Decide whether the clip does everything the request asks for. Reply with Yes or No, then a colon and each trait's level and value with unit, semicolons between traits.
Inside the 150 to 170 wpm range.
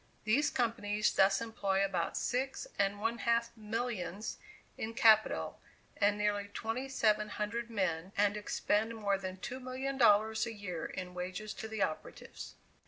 No: average, 140 wpm